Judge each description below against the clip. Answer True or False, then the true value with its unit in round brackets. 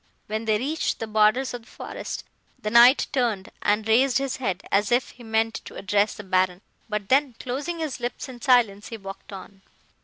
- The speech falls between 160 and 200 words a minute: True (195 wpm)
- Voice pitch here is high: True (225 Hz)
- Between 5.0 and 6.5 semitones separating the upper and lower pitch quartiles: False (3.6 semitones)